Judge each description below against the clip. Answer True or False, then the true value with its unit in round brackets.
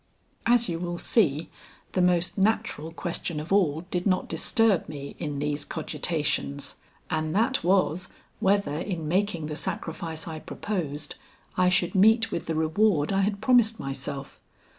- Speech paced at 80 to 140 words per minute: False (150 wpm)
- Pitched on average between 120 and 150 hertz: False (175 Hz)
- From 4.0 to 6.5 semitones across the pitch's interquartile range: True (4.4 semitones)